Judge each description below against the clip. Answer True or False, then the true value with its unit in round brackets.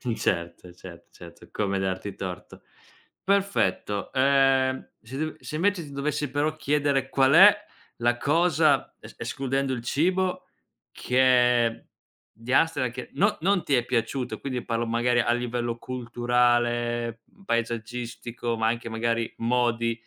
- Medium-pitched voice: False (125 Hz)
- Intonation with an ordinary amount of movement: True (3.2 semitones)